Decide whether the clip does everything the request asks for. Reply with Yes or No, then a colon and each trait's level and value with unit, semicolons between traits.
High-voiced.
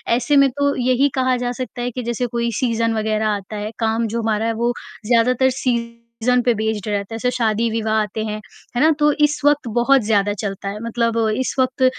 Yes: high, 235 Hz